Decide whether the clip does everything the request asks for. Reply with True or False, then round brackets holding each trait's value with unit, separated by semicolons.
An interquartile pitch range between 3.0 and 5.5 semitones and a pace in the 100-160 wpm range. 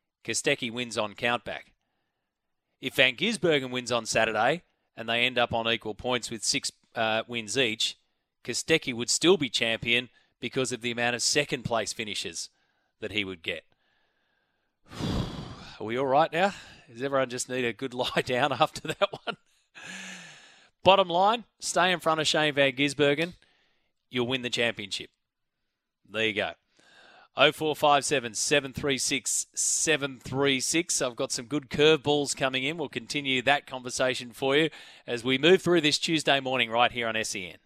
True (3.8 semitones; 155 wpm)